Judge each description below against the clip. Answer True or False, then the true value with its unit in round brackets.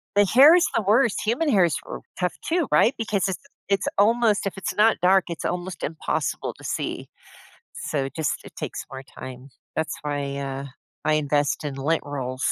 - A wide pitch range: True (6.8 semitones)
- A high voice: False (175 Hz)